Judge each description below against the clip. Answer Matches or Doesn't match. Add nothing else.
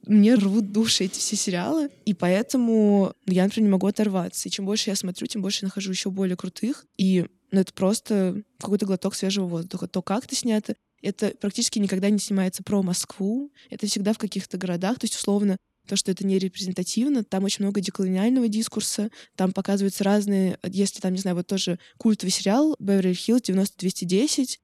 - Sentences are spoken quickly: Matches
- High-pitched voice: Matches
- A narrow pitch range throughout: Matches